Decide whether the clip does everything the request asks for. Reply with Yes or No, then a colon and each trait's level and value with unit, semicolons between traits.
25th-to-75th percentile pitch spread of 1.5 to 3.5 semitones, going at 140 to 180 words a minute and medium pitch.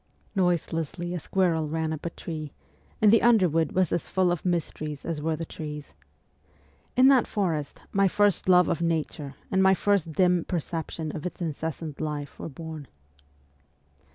Yes: average, 2.9 semitones; average, 160 wpm; medium, 165 Hz